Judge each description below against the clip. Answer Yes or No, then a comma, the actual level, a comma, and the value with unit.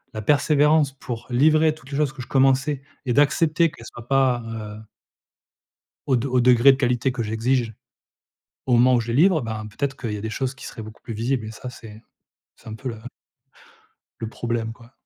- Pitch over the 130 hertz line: No, low, 125 Hz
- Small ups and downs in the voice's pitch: No, average, 3.3 semitones